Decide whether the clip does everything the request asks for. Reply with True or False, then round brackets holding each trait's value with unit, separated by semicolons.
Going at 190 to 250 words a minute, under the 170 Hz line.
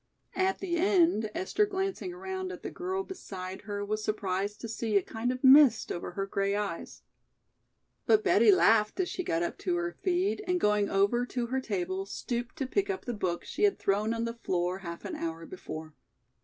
False (200 wpm; 230 Hz)